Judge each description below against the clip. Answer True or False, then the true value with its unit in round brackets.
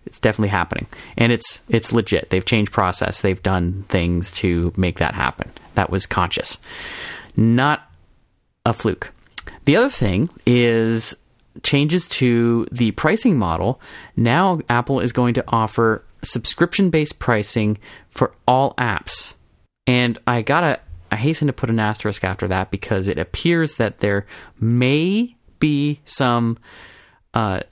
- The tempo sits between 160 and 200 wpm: False (140 wpm)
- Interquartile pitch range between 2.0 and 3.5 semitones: False (4.9 semitones)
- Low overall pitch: True (115 Hz)